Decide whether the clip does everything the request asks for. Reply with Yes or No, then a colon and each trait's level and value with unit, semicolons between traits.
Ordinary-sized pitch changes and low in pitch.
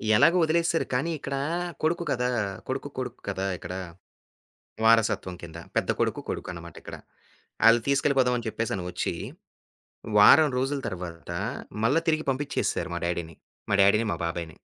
No: wide, 7.9 semitones; low, 115 Hz